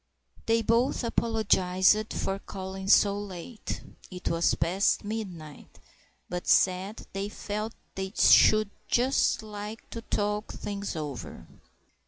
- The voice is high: Yes, high, 200 Hz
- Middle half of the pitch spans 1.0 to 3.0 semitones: Yes, narrow, 2.6 semitones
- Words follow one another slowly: Yes, slow, 115 wpm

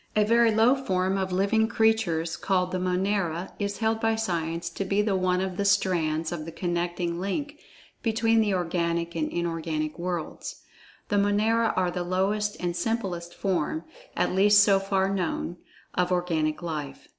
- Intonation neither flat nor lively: Yes, average, 3.2 semitones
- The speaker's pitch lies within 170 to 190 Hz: Yes, medium, 185 Hz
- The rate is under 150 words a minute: No, average, 165 wpm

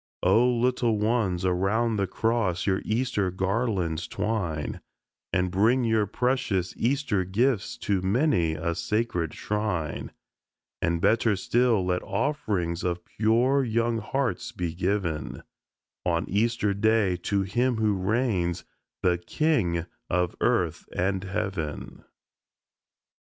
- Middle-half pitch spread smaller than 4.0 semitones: No, average, 4.6 semitones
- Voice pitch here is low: Yes, low, 100 Hz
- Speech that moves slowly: Yes, slow, 115 wpm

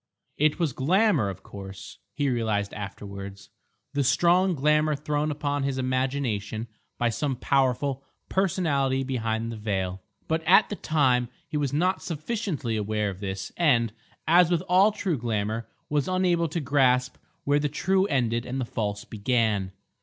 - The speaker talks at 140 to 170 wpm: Yes, average, 155 wpm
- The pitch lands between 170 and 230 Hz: No, low, 135 Hz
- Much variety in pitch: Yes, wide, 5.7 semitones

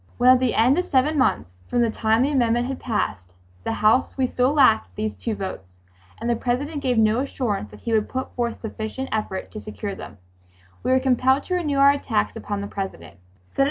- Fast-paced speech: Yes, fast, 210 wpm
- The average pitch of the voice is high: Yes, high, 235 Hz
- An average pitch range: Yes, average, 3.8 semitones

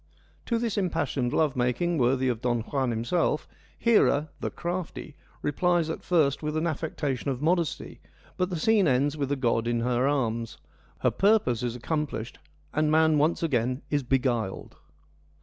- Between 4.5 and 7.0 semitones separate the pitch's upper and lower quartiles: Yes, average, 4.9 semitones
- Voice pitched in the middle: Yes, medium, 145 Hz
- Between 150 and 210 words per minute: Yes, average, 165 wpm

